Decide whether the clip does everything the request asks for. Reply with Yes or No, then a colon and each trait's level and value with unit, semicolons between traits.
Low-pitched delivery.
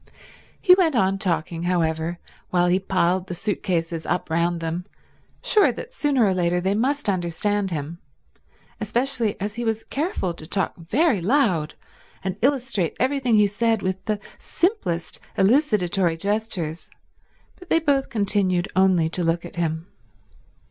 No: high, 190 Hz